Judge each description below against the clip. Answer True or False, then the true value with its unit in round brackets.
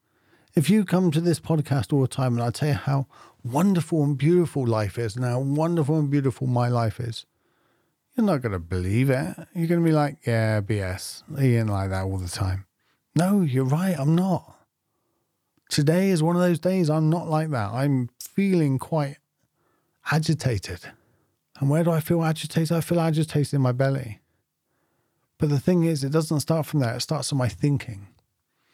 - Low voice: False (145 Hz)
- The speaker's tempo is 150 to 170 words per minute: False (190 wpm)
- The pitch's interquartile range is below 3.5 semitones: False (4.9 semitones)